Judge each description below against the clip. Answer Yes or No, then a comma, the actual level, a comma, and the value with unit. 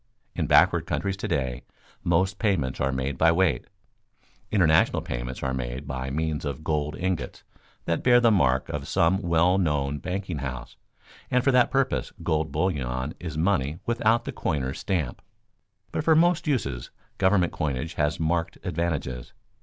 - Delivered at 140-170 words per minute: Yes, average, 155 wpm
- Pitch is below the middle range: Yes, very low, 80 Hz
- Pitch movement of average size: No, wide, 5.9 semitones